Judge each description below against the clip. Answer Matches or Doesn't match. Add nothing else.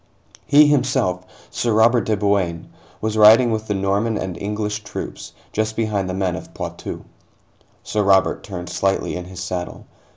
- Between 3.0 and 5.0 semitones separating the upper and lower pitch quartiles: Doesn't match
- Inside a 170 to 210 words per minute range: Doesn't match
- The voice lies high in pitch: Doesn't match